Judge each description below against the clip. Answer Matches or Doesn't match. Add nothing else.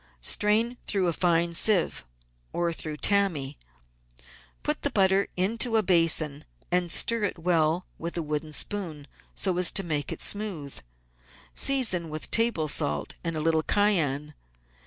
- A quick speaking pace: Doesn't match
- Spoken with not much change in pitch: Doesn't match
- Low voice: Doesn't match